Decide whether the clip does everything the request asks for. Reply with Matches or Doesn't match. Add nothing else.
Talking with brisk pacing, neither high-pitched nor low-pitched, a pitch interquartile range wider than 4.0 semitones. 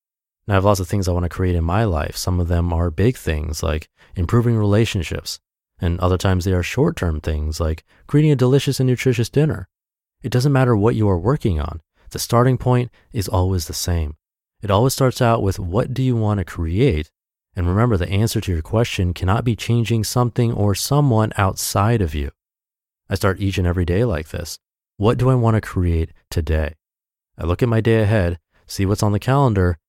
Doesn't match